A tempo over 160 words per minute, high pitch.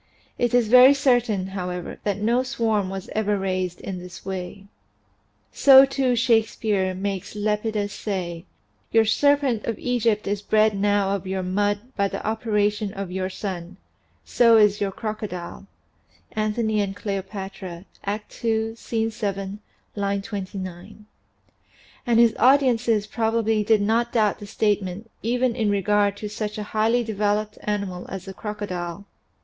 No: average, 145 wpm; high, 210 Hz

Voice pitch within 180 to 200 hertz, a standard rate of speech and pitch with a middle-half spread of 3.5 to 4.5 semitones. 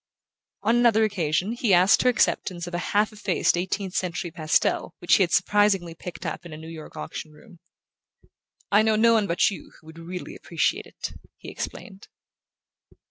Yes: medium, 185 Hz; average, 180 wpm; average, 4.0 semitones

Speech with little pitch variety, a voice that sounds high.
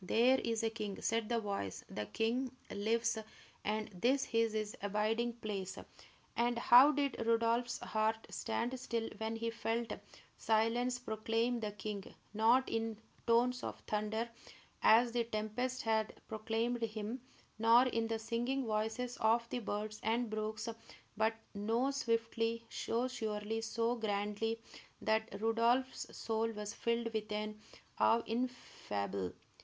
Yes: narrow, 1.6 semitones; high, 225 Hz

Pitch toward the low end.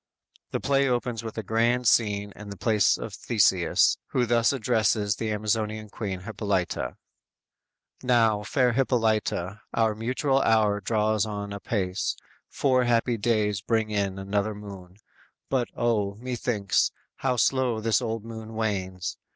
Yes: low, 110 Hz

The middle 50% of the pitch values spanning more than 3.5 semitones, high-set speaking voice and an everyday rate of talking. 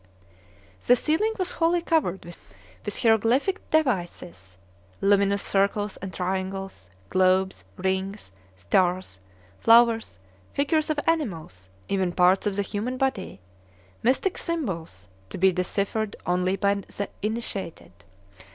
No: average, 4.6 semitones; high, 195 Hz; slow, 110 wpm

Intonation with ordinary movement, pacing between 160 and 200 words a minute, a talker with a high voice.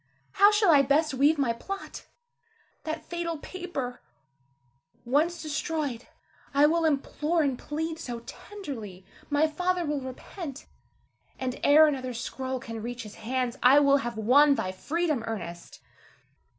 No: average, 4.5 semitones; slow, 135 wpm; very high, 285 Hz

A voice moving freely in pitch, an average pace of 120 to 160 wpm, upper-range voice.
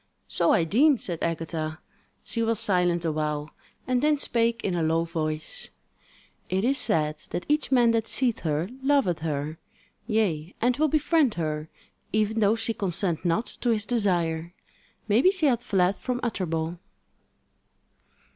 Yes: wide, 6.5 semitones; average, 150 wpm; high, 195 Hz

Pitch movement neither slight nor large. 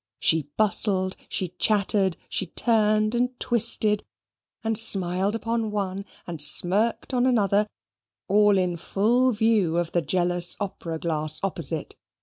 Yes: average, 3.8 semitones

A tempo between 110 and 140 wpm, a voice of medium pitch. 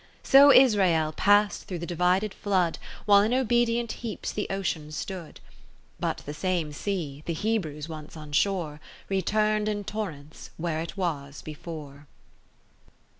Yes: slow, 135 wpm; medium, 180 Hz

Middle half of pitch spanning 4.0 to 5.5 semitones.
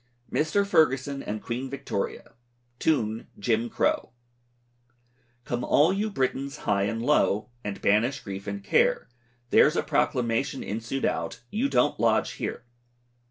Yes: average, 4.7 semitones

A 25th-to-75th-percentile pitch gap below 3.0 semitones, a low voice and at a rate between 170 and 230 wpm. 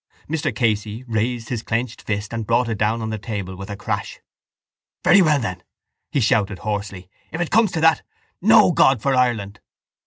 No: average, 3.6 semitones; low, 115 Hz; average, 185 wpm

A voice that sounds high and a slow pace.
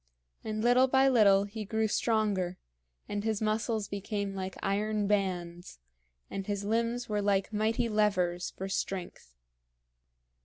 Yes: high, 205 Hz; slow, 130 wpm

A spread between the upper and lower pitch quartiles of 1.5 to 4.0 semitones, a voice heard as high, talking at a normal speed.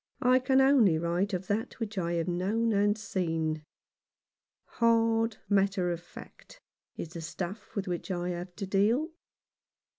No: average, 4.4 semitones; high, 195 Hz; average, 150 wpm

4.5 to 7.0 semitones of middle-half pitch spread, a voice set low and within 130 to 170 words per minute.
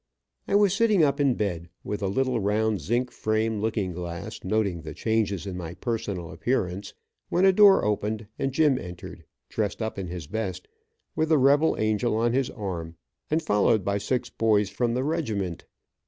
No: average, 5.2 semitones; low, 110 Hz; average, 180 wpm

